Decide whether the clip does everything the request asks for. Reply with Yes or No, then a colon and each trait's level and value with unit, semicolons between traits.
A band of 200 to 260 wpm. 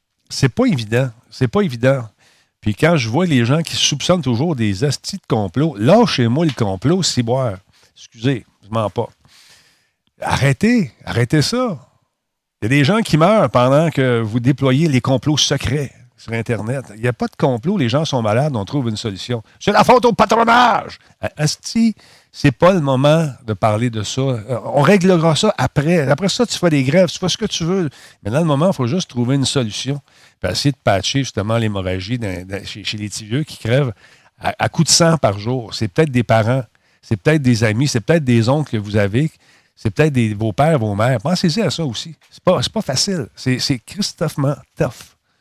Yes: average, 205 wpm